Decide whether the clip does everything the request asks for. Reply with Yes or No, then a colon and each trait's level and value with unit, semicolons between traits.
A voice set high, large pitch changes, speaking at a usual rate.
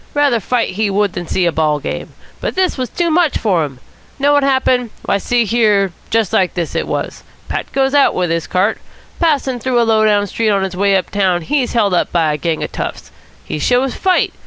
No: high, 215 Hz; wide, 6.0 semitones; fast, 230 wpm